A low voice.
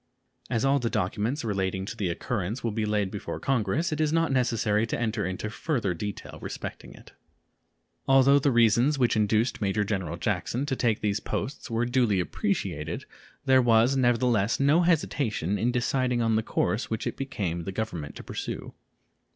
Yes: low, 115 Hz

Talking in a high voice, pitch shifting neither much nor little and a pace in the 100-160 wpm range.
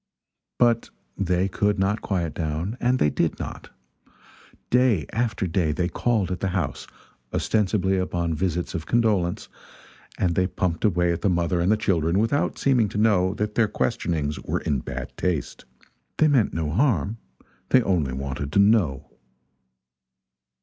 No: very low, 95 Hz; average, 4.4 semitones; average, 155 wpm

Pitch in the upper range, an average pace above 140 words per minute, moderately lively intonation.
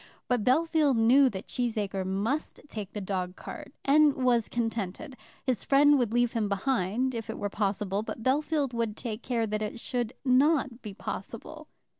Yes: high, 235 Hz; average, 170 wpm; average, 4.0 semitones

